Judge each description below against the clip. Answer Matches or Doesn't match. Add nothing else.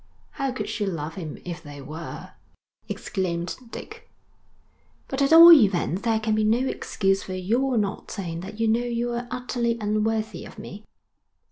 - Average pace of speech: Matches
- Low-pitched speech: Doesn't match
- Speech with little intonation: Doesn't match